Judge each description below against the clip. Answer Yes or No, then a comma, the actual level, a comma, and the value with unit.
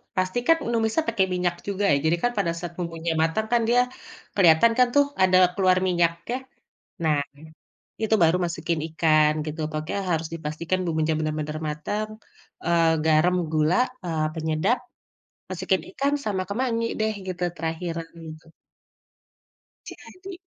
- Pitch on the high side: No, medium, 170 Hz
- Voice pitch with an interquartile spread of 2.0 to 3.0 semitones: No, average, 4.3 semitones